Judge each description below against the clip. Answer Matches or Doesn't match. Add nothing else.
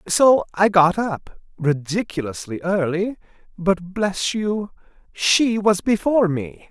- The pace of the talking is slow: Matches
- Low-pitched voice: Doesn't match